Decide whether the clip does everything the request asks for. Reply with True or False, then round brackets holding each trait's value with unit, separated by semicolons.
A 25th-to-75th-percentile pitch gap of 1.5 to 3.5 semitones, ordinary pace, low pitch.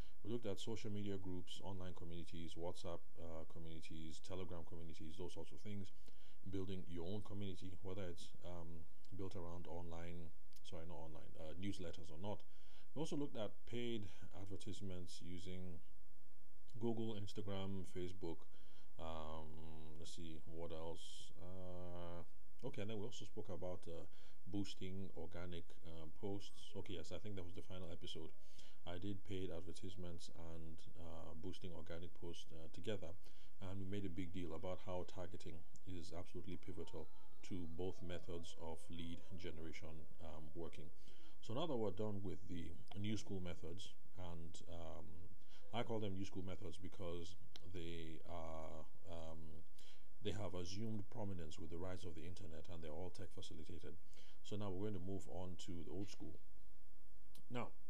True (3.0 semitones; 155 wpm; 90 Hz)